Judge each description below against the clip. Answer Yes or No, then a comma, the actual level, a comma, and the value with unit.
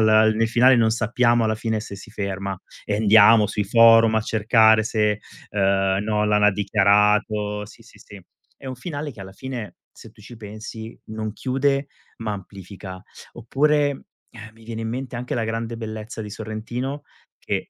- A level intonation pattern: Yes, narrow, 2.1 semitones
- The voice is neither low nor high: No, low, 110 Hz